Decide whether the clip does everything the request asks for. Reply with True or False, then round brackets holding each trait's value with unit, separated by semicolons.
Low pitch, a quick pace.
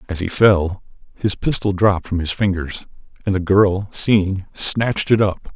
False (100 Hz; 175 wpm)